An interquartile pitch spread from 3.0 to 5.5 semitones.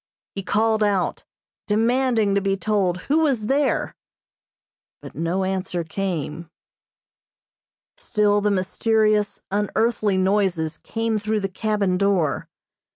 No: narrow, 2.5 semitones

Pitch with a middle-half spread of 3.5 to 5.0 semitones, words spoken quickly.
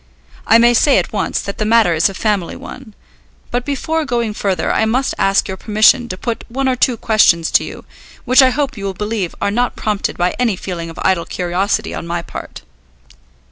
Yes: average, 4.4 semitones; fast, 210 wpm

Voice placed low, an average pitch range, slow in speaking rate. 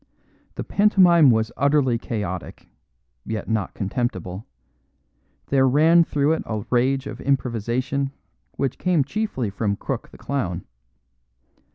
Yes: low, 130 Hz; average, 4.5 semitones; slow, 115 wpm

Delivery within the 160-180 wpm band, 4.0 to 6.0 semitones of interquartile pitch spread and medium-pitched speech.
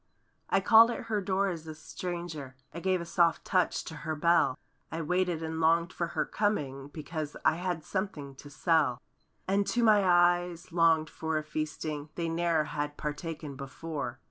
No: average, 170 wpm; average, 2.7 semitones; medium, 165 Hz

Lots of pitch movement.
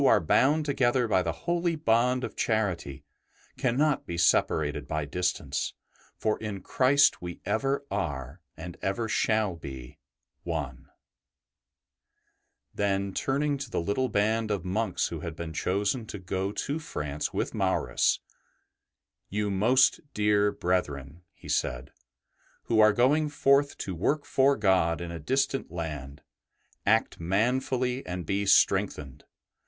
Yes: wide, 7.0 semitones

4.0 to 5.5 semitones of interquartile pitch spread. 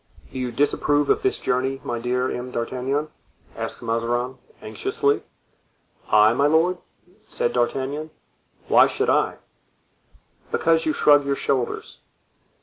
No: average, 3.2 semitones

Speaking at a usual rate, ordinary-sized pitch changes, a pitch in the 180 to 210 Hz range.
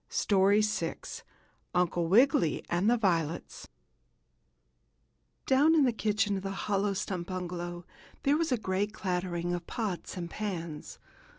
No: slow, 130 wpm; average, 3.5 semitones; high, 190 Hz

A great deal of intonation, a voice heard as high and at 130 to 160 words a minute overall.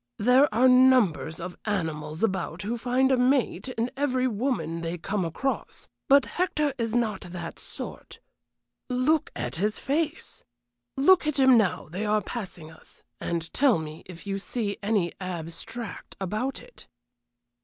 Yes: wide, 6.7 semitones; high, 215 Hz; average, 150 wpm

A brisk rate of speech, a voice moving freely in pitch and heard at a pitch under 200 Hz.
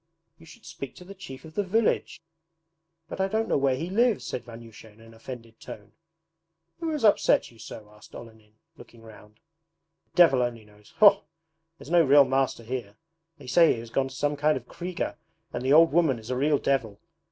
Yes: fast, 210 wpm; wide, 6.4 semitones; low, 135 Hz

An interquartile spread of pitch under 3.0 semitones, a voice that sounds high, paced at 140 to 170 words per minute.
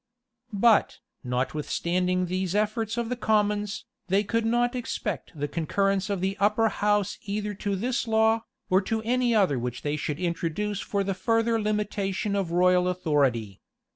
No: average, 3.4 semitones; high, 200 Hz; average, 155 wpm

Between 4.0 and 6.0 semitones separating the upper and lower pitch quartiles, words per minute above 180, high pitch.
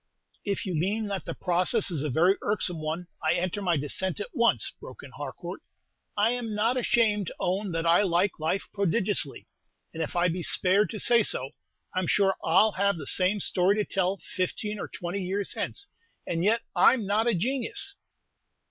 No: average, 3.4 semitones; average, 200 wpm; high, 195 Hz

